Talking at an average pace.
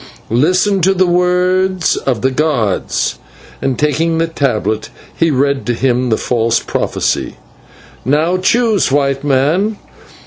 No: slow, 130 wpm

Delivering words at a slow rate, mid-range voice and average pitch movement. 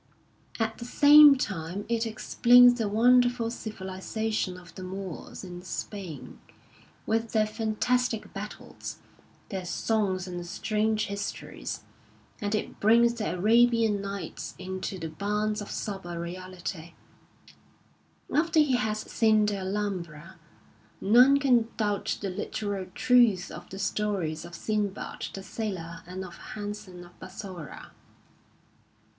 No: slow, 120 wpm; high, 205 Hz; average, 3.2 semitones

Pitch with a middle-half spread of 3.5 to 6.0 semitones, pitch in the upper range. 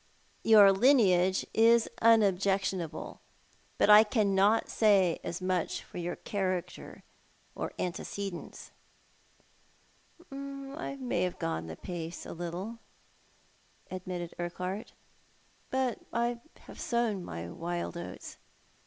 Yes: average, 4.4 semitones; high, 195 Hz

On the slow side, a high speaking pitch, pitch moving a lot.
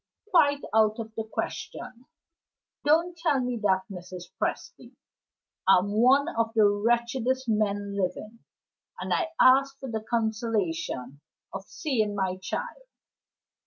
No: slow, 125 wpm; high, 220 Hz; average, 4.4 semitones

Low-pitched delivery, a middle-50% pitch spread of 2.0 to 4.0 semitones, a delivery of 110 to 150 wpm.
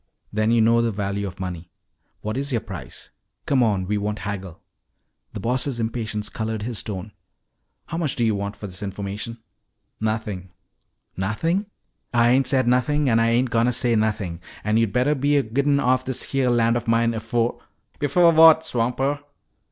No: low, 115 Hz; average, 3.6 semitones; average, 185 wpm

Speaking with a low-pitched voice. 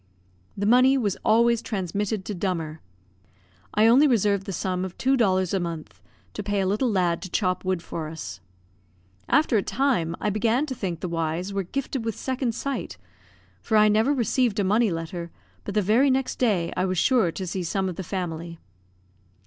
No: high, 200 Hz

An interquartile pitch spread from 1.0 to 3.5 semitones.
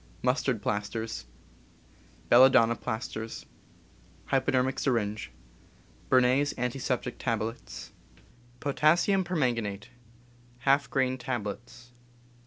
Yes: average, 2.8 semitones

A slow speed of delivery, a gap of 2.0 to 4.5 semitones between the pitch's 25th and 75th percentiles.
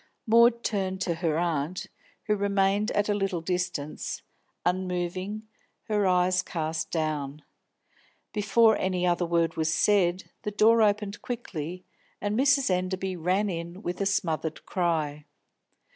Yes: slow, 130 wpm; average, 3.4 semitones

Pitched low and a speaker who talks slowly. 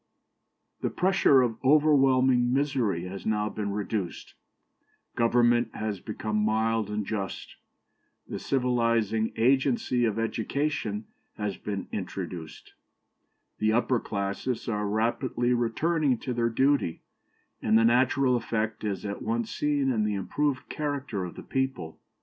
Yes: low, 115 Hz; slow, 125 wpm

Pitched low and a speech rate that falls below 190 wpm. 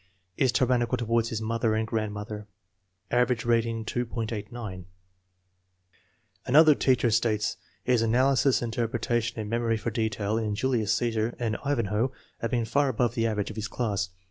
Yes: low, 115 Hz; average, 155 wpm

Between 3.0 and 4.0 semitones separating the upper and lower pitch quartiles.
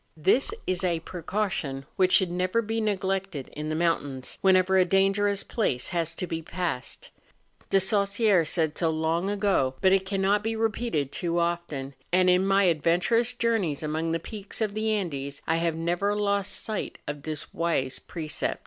Yes: average, 3.7 semitones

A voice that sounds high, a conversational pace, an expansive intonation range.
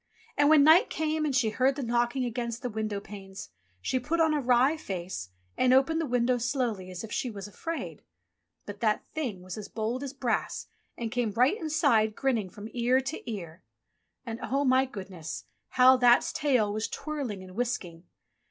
No: high, 240 Hz; average, 185 wpm; average, 4.4 semitones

